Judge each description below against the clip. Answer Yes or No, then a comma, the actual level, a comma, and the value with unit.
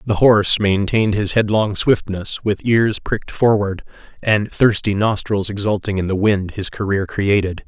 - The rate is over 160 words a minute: No, average, 155 wpm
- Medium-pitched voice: No, low, 100 Hz